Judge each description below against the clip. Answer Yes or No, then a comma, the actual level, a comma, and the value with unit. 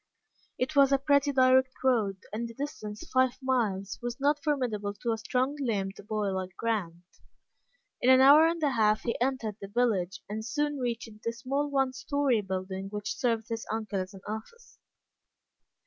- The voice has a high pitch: Yes, high, 235 Hz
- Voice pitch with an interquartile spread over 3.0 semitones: Yes, average, 4.4 semitones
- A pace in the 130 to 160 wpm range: No, average, 175 wpm